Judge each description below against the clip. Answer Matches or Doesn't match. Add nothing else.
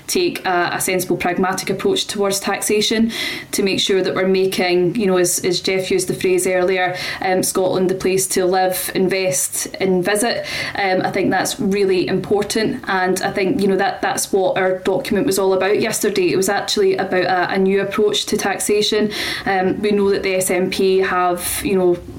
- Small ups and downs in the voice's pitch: Matches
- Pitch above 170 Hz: Matches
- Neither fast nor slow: Matches